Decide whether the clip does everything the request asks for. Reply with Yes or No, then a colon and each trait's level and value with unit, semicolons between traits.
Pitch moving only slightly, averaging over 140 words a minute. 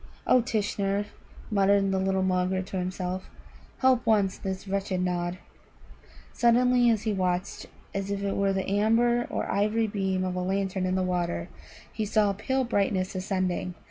Yes: narrow, 2.2 semitones; average, 165 wpm